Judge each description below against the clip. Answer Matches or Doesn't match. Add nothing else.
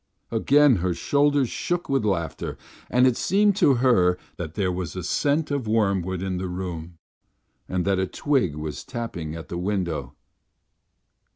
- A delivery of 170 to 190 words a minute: Doesn't match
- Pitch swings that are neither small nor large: Doesn't match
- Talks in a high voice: Doesn't match